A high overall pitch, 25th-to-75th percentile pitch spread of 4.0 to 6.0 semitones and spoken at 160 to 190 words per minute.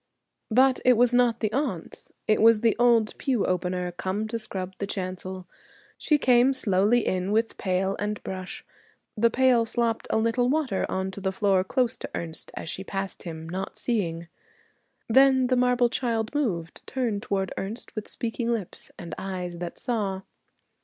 Yes: high, 215 Hz; average, 4.4 semitones; average, 170 wpm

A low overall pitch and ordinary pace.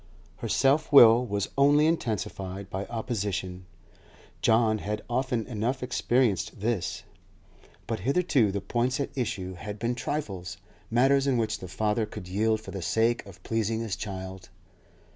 Yes: low, 110 Hz; average, 145 wpm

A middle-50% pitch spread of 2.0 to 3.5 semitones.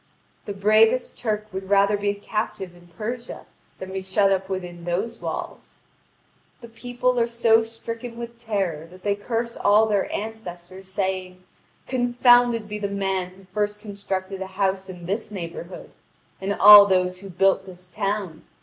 Yes: average, 2.9 semitones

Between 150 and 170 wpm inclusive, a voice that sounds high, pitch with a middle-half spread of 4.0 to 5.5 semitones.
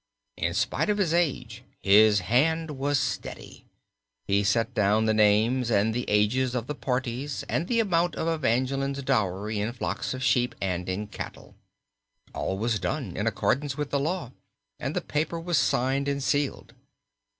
No: average, 165 wpm; low, 130 Hz; average, 5.1 semitones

